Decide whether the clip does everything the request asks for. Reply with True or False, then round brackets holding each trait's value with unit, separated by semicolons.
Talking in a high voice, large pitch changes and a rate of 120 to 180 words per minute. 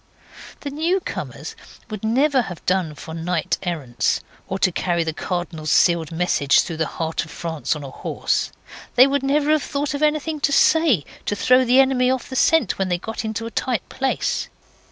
False (220 Hz; 8.6 semitones; 190 wpm)